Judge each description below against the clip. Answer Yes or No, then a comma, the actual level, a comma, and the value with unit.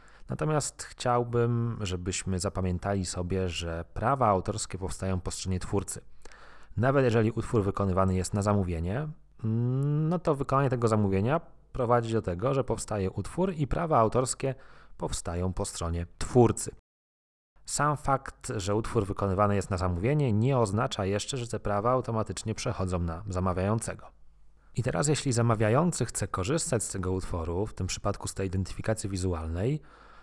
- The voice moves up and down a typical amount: Yes, average, 5.0 semitones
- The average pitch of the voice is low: Yes, low, 105 Hz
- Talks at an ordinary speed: Yes, average, 140 wpm